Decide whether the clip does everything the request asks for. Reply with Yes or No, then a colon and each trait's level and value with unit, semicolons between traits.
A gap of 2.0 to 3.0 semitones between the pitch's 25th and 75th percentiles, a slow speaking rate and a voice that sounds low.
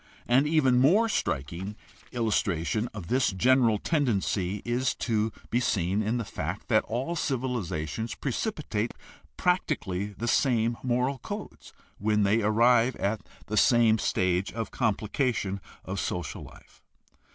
No: average, 3.9 semitones; slow, 130 wpm; low, 115 Hz